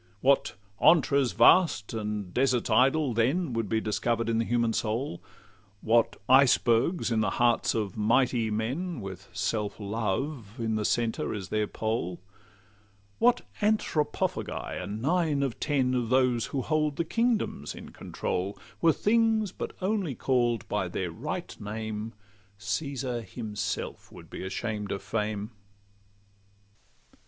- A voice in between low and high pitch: No, low, 115 Hz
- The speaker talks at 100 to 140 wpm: Yes, slow, 135 wpm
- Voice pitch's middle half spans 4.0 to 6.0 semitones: Yes, average, 4.6 semitones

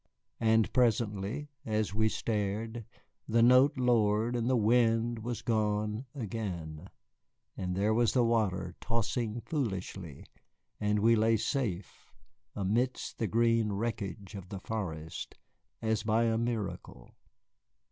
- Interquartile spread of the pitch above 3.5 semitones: No, narrow, 2.5 semitones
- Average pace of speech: No, slow, 120 wpm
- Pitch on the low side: Yes, low, 110 Hz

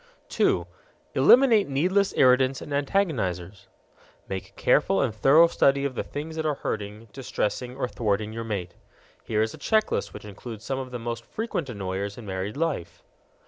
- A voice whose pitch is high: No, low, 125 Hz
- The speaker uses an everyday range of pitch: No, wide, 5.7 semitones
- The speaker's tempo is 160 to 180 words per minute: Yes, average, 175 wpm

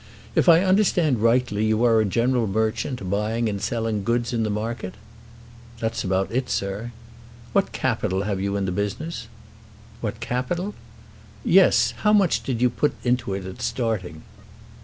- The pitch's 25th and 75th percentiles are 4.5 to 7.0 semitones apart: No, average, 3.8 semitones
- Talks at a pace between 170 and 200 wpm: No, average, 160 wpm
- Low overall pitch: Yes, low, 115 Hz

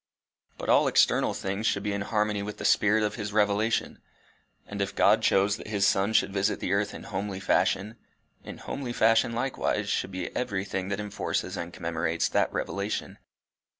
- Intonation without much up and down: Yes, narrow, 1.8 semitones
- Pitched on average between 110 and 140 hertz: No, low, 100 Hz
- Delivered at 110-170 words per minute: No, average, 180 wpm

